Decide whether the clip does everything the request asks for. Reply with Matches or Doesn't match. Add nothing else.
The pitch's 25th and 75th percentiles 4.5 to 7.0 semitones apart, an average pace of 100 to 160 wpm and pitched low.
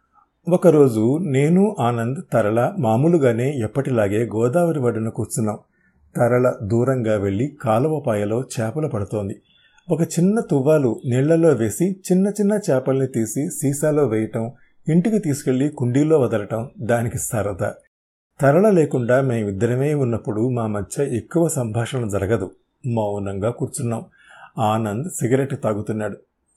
Matches